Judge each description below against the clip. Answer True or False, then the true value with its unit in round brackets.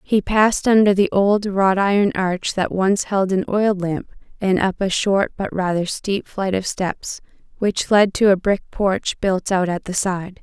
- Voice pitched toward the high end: True (195 Hz)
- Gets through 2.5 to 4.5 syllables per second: True (4.2 syllables/s)